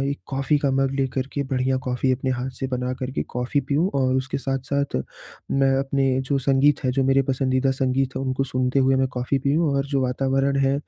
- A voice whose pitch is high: No, low, 135 Hz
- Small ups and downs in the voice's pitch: Yes, narrow, 1.1 semitones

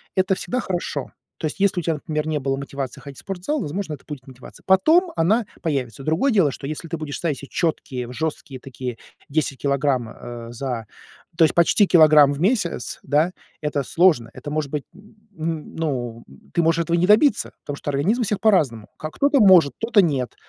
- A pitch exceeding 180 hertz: No, medium, 155 Hz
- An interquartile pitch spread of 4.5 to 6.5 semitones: Yes, average, 5.3 semitones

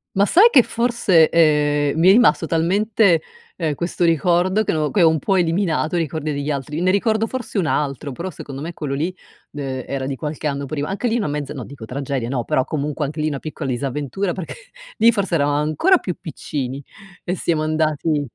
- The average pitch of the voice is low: No, medium, 155 Hz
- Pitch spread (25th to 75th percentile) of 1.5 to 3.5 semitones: No, average, 4.4 semitones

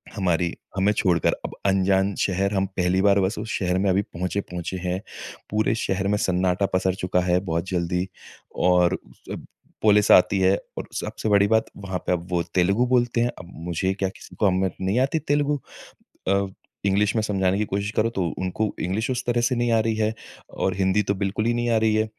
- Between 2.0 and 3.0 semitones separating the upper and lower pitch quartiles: Yes, average, 2.7 semitones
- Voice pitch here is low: Yes, low, 100 Hz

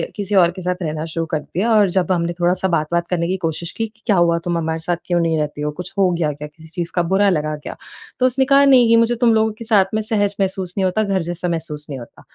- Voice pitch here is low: No, medium, 180 Hz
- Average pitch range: Yes, average, 3.8 semitones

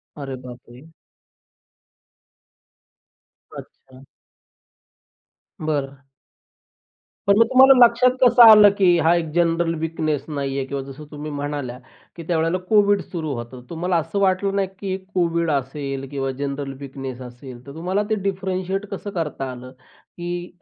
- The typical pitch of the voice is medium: Yes, medium, 160 Hz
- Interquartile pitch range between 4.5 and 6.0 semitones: Yes, wide, 5.4 semitones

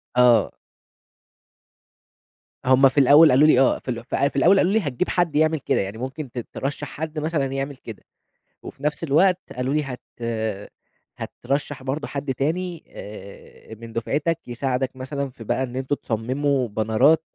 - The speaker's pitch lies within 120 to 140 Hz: Yes, low, 135 Hz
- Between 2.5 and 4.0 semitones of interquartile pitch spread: Yes, average, 3.4 semitones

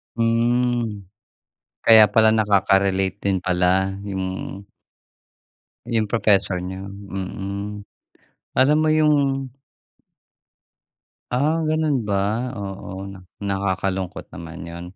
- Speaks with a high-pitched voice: No, low, 100 Hz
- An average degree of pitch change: Yes, average, 3.3 semitones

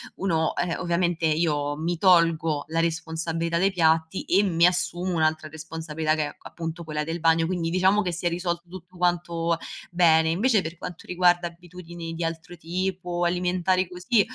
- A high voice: No, medium, 170 Hz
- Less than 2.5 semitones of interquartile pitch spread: Yes, narrow, 1.7 semitones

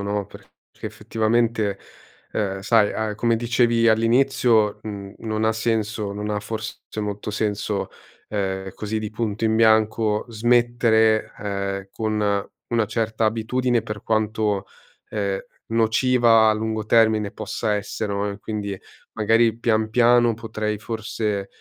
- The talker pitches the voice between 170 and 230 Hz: No, low, 110 Hz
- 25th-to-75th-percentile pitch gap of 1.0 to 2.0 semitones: Yes, narrow, 1.6 semitones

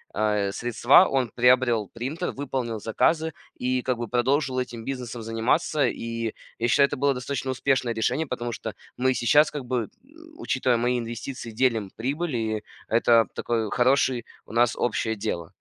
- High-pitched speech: No, low, 125 Hz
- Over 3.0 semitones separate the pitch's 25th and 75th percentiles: No, average, 2.7 semitones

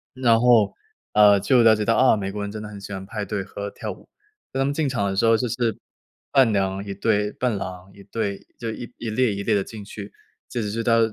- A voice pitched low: Yes, low, 105 Hz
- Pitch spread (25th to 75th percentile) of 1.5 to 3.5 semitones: Yes, narrow, 2.4 semitones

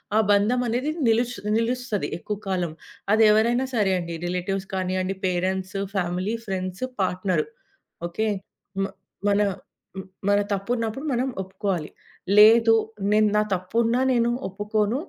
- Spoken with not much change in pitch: No, average, 3.7 semitones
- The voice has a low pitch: No, high, 205 Hz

